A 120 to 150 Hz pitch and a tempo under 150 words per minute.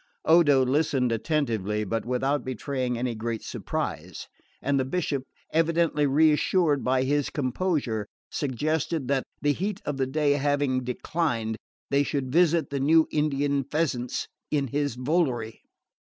Yes: medium, 140 Hz; slow, 135 wpm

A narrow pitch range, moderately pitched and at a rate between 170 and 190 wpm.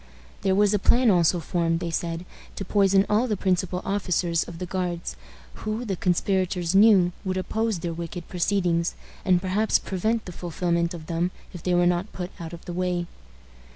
Yes: narrow, 2.3 semitones; medium, 180 Hz; average, 185 wpm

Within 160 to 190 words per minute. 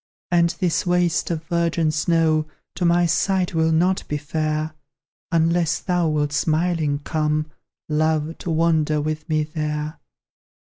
No: slow, 135 wpm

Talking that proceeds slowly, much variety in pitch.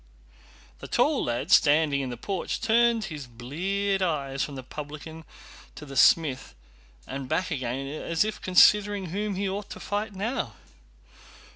No: average, 150 wpm; wide, 6.4 semitones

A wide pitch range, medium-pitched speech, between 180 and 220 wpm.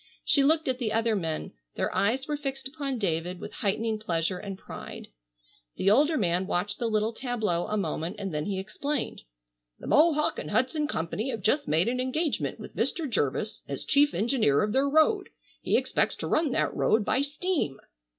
No: wide, 6.6 semitones; high, 225 Hz; average, 190 wpm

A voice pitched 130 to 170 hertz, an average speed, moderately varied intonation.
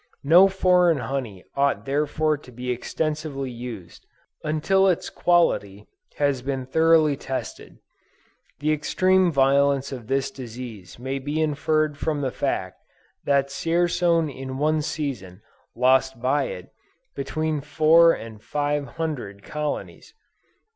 No: medium, 140 Hz; slow, 120 wpm; average, 3.2 semitones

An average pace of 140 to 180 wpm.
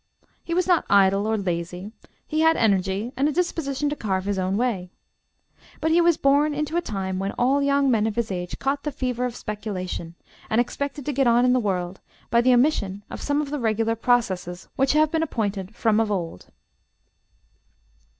No: average, 200 wpm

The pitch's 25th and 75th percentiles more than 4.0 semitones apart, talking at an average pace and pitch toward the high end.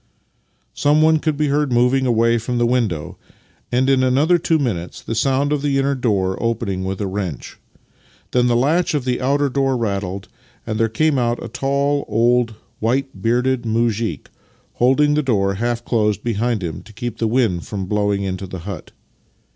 No: average, 4.5 semitones; average, 180 wpm; low, 120 Hz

